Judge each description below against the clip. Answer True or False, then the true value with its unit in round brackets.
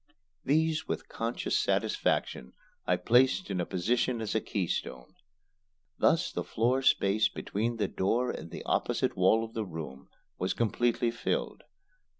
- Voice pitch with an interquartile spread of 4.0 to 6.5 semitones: True (4.5 semitones)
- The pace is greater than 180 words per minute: False (140 wpm)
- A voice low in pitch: True (115 Hz)